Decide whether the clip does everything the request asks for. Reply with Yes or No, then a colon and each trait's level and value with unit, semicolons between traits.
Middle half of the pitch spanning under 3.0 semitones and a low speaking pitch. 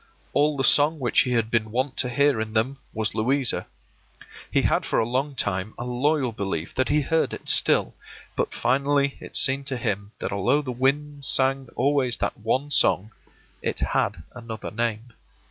No: average, 3.9 semitones; low, 125 Hz